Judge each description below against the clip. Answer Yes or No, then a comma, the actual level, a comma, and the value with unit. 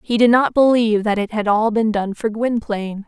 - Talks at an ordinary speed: No, fast, 235 wpm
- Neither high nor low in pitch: No, high, 220 Hz